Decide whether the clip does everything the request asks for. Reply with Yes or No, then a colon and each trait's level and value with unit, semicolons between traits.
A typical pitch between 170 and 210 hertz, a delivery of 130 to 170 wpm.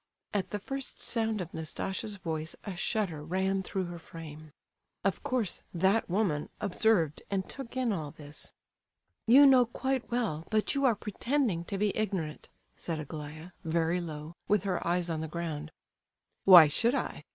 Yes: medium, 185 Hz; average, 165 wpm